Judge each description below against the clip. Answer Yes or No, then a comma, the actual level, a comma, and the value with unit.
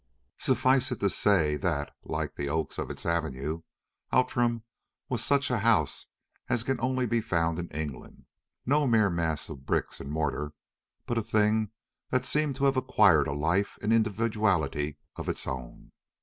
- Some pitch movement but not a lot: No, wide, 7.6 semitones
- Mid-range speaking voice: No, low, 105 Hz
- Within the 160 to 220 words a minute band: Yes, average, 165 wpm